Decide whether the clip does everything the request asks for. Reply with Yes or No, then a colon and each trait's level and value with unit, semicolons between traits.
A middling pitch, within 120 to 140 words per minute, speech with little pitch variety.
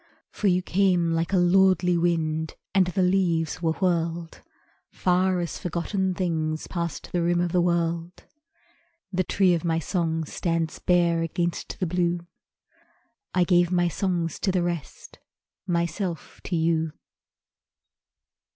Yes: medium, 175 Hz; slow, 135 wpm; narrow, 1.5 semitones